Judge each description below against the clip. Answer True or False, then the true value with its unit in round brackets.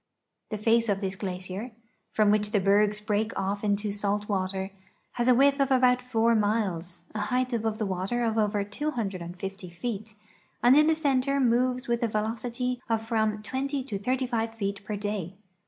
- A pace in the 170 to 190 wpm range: True (175 wpm)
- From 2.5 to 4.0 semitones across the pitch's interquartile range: True (3.4 semitones)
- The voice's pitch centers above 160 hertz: True (215 Hz)